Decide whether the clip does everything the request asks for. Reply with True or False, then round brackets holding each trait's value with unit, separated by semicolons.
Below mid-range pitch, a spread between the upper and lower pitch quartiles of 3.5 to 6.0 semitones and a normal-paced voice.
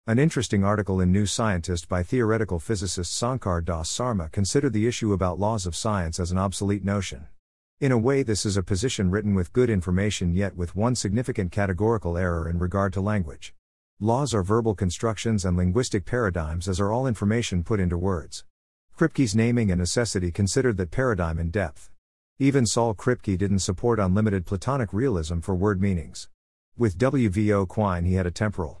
True (100 Hz; 4.0 semitones; 180 wpm)